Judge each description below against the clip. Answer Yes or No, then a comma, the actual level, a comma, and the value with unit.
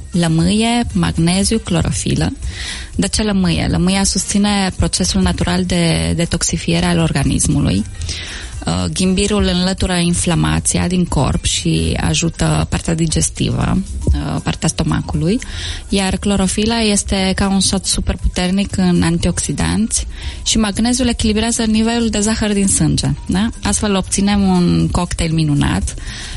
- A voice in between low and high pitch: Yes, medium, 170 Hz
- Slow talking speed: Yes, slow, 110 wpm